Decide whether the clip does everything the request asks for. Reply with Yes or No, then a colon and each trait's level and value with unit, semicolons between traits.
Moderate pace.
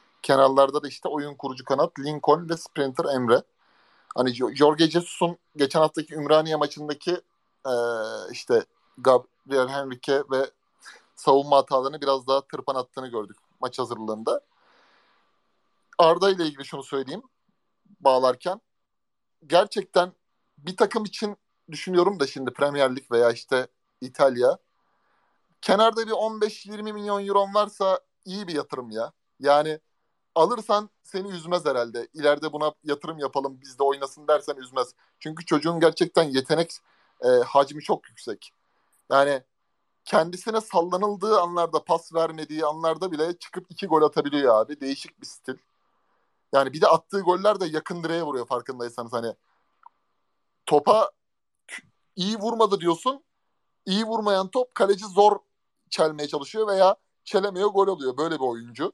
Yes: average, 130 wpm